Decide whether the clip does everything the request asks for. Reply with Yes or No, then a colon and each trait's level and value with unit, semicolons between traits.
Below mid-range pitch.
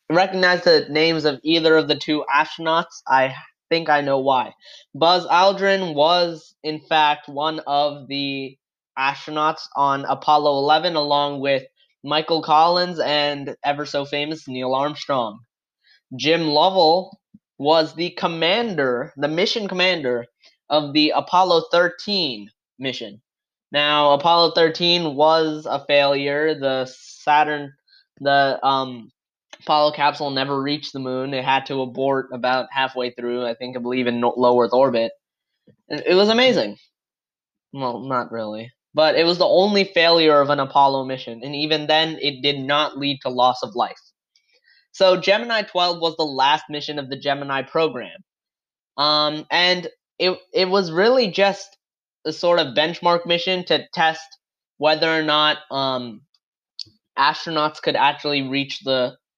No: medium, 150 Hz